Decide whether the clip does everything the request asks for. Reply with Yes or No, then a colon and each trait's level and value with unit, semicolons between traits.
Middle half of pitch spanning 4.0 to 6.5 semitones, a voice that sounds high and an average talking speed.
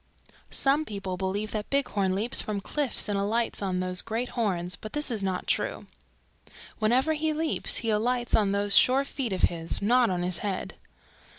Yes: average, 4.6 semitones; high, 215 Hz; average, 175 wpm